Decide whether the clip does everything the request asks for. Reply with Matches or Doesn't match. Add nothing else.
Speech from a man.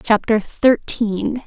Doesn't match